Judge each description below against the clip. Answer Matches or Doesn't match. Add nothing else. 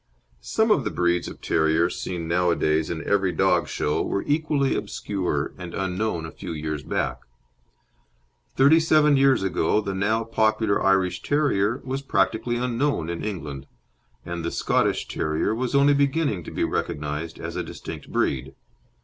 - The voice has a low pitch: Matches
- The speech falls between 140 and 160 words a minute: Matches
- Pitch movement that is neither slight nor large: Doesn't match